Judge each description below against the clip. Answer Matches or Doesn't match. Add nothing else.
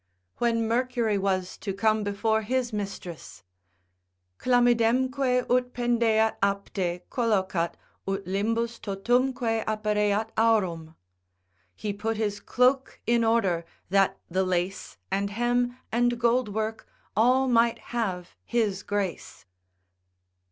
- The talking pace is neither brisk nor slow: Doesn't match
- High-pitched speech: Matches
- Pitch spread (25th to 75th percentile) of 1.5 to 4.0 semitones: Matches